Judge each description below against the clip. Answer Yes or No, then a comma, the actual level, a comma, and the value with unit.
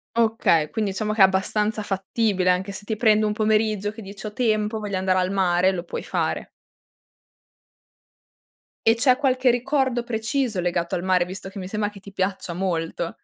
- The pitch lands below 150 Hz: No, high, 205 Hz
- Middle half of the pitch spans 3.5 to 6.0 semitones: No, average, 2.8 semitones